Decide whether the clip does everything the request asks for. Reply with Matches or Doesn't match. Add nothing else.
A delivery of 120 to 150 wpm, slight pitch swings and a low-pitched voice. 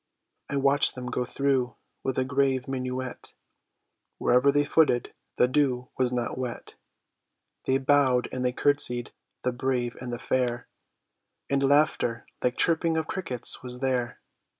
Matches